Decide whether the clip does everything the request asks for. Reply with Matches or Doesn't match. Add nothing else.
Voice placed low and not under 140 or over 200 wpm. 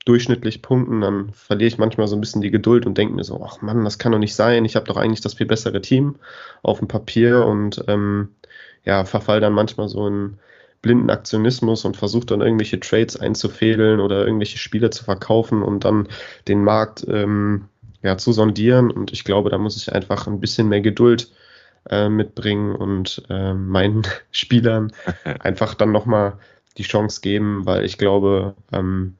Matches